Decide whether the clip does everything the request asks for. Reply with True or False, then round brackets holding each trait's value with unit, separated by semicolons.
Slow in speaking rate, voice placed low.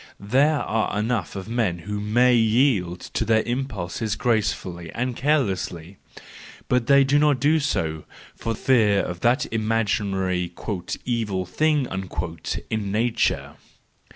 True (130 wpm; 110 Hz)